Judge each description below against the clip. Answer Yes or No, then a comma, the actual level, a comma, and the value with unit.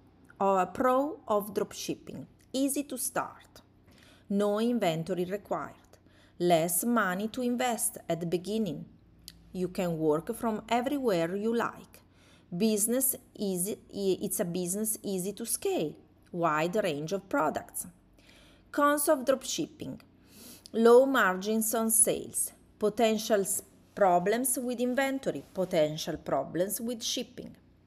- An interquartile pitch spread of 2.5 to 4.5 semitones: No, average, 5.1 semitones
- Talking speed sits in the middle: No, slow, 110 wpm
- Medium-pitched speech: No, high, 215 Hz